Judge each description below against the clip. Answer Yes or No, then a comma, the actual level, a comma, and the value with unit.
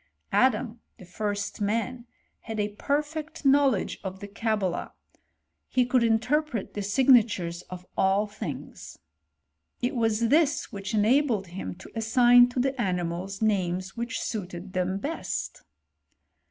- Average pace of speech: No, slow, 130 wpm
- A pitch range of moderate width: Yes, average, 4.5 semitones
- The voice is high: Yes, high, 215 Hz